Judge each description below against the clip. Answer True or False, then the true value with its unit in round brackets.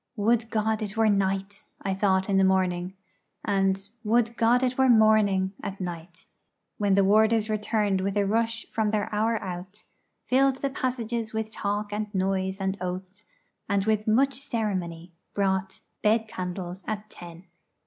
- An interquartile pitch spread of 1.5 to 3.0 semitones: True (2.6 semitones)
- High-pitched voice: True (205 Hz)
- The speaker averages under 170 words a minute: True (160 wpm)